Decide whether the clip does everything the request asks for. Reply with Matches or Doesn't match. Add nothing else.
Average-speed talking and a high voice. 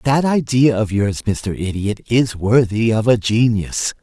Doesn't match